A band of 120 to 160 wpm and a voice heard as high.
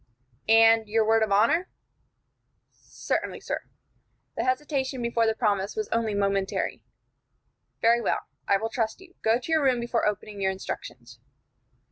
Yes: average, 145 wpm; high, 225 Hz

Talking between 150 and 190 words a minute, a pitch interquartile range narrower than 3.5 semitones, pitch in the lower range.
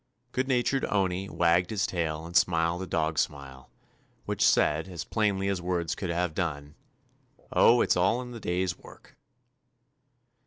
Yes: average, 160 wpm; average, 3.0 semitones; very low, 90 Hz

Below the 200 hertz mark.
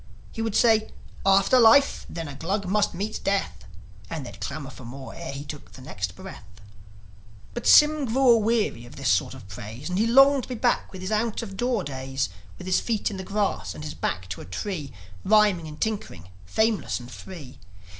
Yes: high, 190 Hz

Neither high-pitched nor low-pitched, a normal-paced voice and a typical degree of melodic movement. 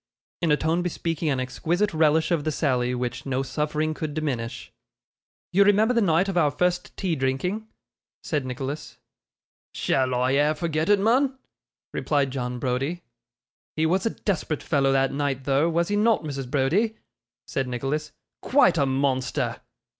Yes: medium, 150 Hz; average, 160 wpm; average, 4.7 semitones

